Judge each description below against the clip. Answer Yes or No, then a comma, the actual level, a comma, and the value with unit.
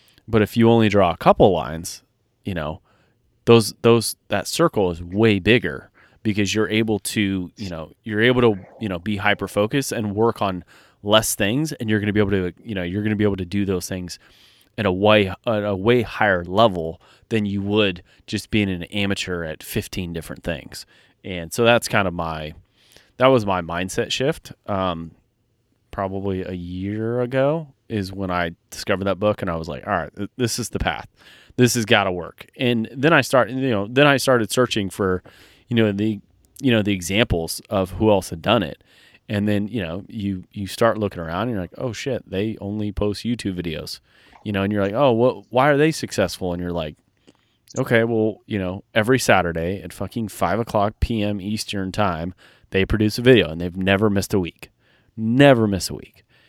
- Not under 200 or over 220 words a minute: Yes, fast, 205 wpm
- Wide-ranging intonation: No, average, 3.6 semitones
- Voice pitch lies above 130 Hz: No, low, 105 Hz